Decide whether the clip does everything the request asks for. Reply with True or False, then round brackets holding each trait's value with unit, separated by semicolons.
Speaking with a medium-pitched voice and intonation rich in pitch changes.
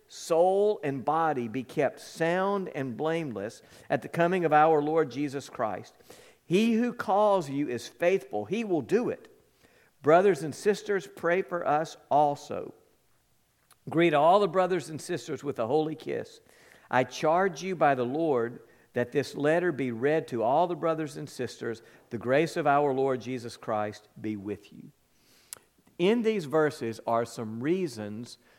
True (155 Hz; 6.1 semitones)